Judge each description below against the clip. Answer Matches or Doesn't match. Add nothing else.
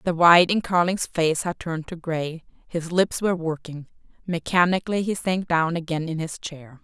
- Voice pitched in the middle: Matches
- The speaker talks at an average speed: Matches